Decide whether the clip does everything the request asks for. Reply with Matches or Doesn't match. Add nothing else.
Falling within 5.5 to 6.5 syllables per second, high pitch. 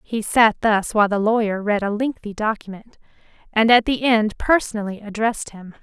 Doesn't match